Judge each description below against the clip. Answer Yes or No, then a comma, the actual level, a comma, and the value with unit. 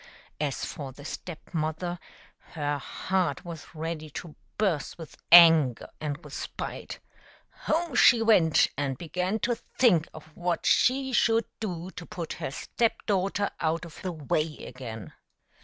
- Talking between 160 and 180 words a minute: No, average, 145 wpm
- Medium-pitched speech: Yes, medium, 165 Hz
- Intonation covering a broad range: No, average, 4.0 semitones